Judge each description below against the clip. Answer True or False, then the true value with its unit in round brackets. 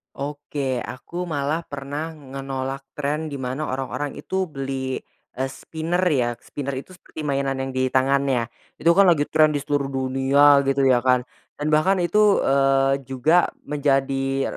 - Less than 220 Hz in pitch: True (140 Hz)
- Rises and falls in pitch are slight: True (2.2 semitones)